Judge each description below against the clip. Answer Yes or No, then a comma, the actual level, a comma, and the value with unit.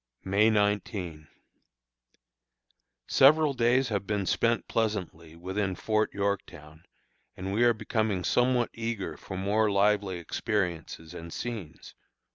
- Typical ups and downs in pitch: Yes, average, 3.5 semitones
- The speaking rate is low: Yes, slow, 110 wpm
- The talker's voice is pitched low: Yes, low, 105 Hz